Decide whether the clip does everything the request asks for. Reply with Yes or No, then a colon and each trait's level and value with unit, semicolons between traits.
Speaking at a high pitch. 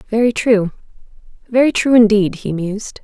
Yes: high, 215 Hz